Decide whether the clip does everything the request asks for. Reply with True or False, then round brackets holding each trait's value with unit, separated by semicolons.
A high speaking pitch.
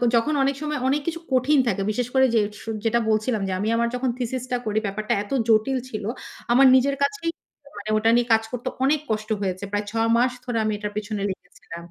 True (230 Hz)